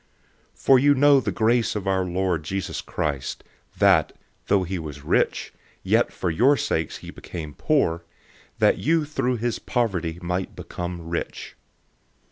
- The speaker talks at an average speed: Yes, average, 150 wpm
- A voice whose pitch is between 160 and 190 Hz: No, very low, 95 Hz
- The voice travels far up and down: Yes, wide, 6.7 semitones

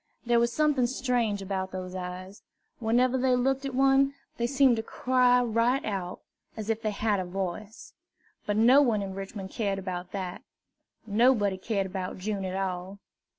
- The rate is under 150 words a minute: No, average, 170 wpm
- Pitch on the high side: Yes, high, 215 Hz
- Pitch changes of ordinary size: Yes, average, 4.6 semitones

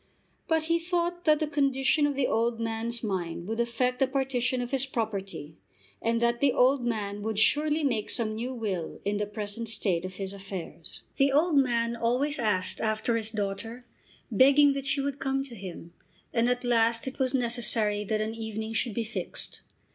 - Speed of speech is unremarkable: Yes, average, 190 wpm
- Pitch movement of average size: Yes, average, 3.9 semitones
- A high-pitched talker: Yes, high, 235 Hz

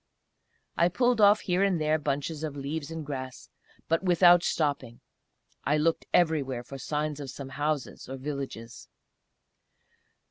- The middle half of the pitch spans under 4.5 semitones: Yes, average, 3.3 semitones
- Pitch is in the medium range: Yes, medium, 150 Hz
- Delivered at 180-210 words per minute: No, average, 140 wpm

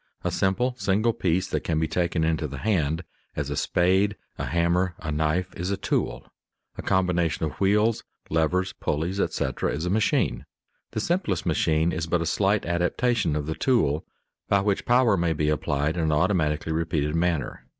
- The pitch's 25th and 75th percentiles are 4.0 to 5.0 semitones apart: No, average, 3.6 semitones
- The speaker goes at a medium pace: Yes, average, 180 wpm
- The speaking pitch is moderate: No, very low, 85 Hz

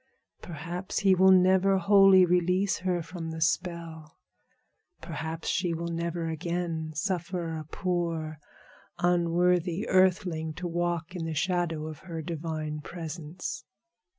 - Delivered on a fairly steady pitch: Yes, narrow, 2.1 semitones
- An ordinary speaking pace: No, slow, 125 wpm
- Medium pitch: Yes, medium, 170 Hz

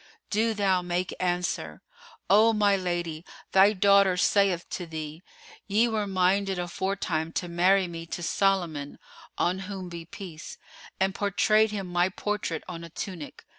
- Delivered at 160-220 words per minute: No, average, 145 wpm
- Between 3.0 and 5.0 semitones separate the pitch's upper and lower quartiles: No, narrow, 2.4 semitones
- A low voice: No, medium, 185 Hz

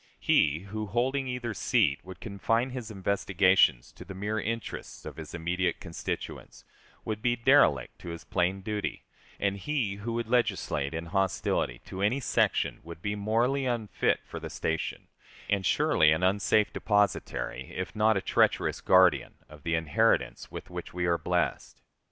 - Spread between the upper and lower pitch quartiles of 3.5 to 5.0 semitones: Yes, average, 4.6 semitones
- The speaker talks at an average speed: Yes, average, 160 wpm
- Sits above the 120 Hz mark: No, low, 100 Hz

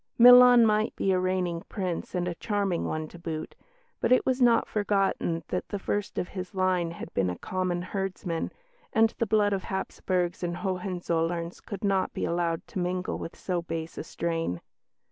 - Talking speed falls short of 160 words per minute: No, average, 185 wpm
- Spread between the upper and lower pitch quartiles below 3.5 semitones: Yes, average, 3.0 semitones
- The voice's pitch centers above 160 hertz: Yes, medium, 185 Hz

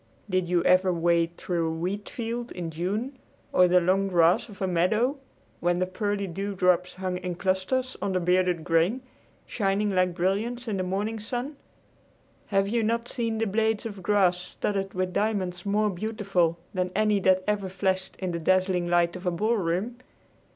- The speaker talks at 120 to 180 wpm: Yes, average, 175 wpm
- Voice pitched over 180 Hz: Yes, high, 190 Hz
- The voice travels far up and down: No, average, 2.9 semitones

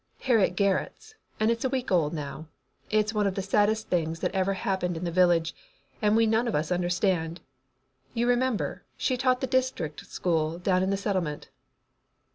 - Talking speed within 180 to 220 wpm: Yes, average, 185 wpm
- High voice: Yes, high, 195 Hz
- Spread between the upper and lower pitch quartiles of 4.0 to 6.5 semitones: Yes, average, 4.5 semitones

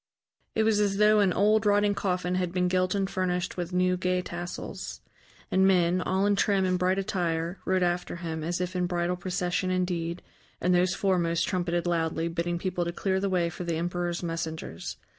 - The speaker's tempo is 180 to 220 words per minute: Yes, average, 195 wpm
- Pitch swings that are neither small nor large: No, narrow, 1.5 semitones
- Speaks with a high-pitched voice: No, medium, 180 Hz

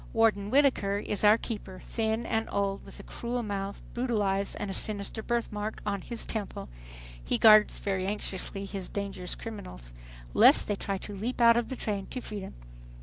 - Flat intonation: Yes, narrow, 2.3 semitones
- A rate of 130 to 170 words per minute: No, average, 180 wpm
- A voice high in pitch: Yes, high, 210 Hz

